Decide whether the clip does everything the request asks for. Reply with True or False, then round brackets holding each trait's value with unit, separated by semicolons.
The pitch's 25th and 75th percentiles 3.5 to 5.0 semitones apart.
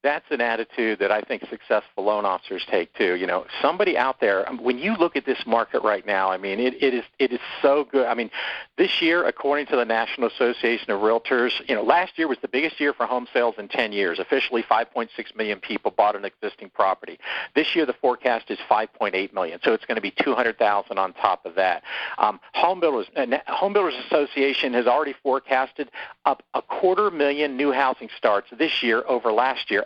True (4.0 semitones)